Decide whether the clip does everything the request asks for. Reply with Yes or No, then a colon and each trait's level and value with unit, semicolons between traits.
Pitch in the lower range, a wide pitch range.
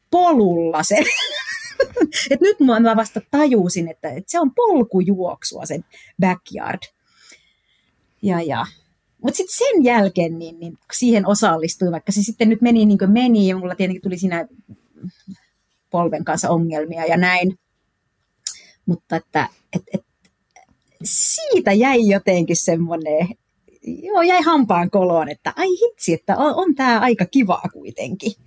No: high, 200 Hz; wide, 6.4 semitones